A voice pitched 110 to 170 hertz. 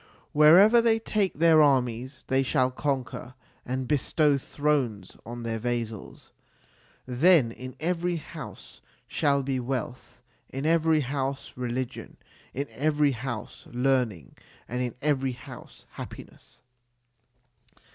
Yes: low, 135 Hz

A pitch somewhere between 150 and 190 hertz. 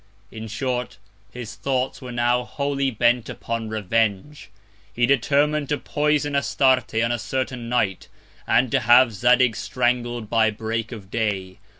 No: low, 120 Hz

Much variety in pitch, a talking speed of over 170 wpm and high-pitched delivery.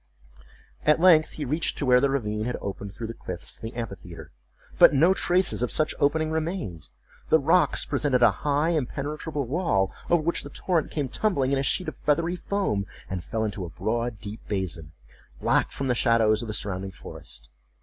No: wide, 6.8 semitones; average, 190 wpm; low, 130 Hz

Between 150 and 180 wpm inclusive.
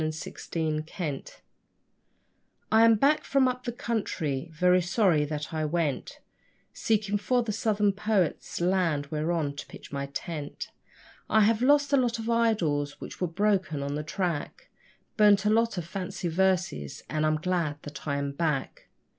Yes: average, 165 wpm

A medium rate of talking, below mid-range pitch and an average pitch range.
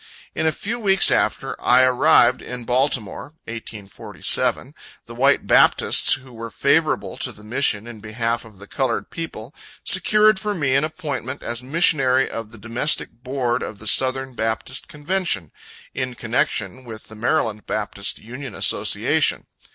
Yes: average, 150 wpm; low, 125 Hz; average, 4.1 semitones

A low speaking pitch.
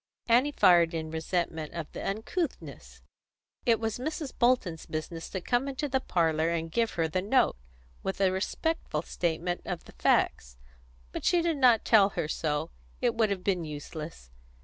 No: medium, 185 Hz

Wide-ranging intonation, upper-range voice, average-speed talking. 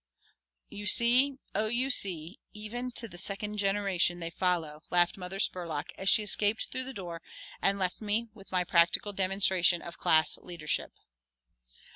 No: average, 3.3 semitones; high, 195 Hz; average, 155 wpm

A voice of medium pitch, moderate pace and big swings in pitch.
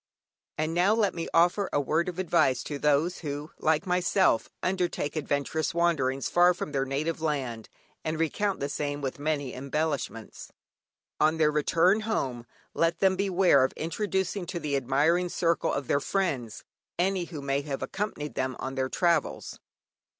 No: medium, 155 Hz; average, 160 wpm; average, 4.1 semitones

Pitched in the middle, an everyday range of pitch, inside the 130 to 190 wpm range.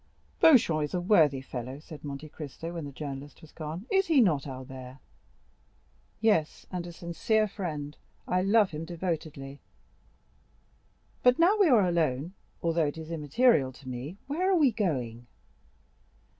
No: medium, 160 Hz; wide, 5.9 semitones; average, 145 wpm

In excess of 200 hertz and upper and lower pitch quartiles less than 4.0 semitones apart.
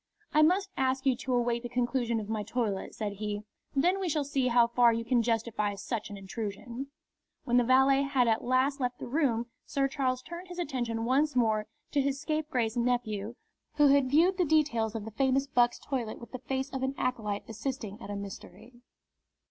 Yes: high, 245 Hz; average, 3.4 semitones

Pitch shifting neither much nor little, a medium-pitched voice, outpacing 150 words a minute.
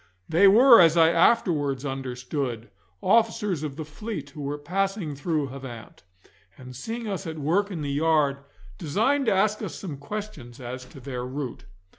No: wide, 6.2 semitones; medium, 155 Hz; average, 165 wpm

